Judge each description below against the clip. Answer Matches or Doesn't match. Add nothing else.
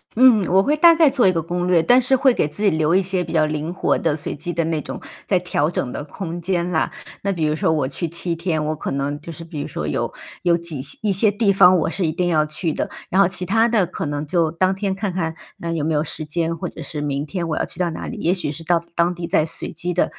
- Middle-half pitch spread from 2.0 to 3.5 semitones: Matches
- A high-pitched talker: Doesn't match